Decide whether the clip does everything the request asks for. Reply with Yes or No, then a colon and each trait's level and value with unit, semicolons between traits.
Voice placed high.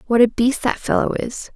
Yes: high, 245 Hz